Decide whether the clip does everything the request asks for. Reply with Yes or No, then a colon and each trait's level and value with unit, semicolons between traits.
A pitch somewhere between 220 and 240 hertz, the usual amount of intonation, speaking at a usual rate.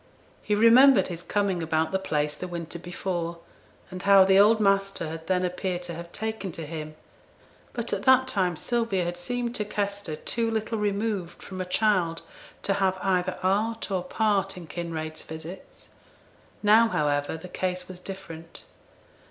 No: medium, 185 Hz; average, 3.3 semitones; average, 165 wpm